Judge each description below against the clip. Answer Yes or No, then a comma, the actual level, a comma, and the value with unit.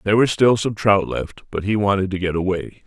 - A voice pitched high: No, low, 100 Hz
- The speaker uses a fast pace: Yes, fast, 250 wpm